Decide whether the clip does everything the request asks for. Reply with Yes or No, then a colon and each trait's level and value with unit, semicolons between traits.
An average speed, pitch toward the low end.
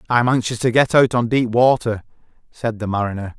Yes: average, 195 wpm; low, 115 Hz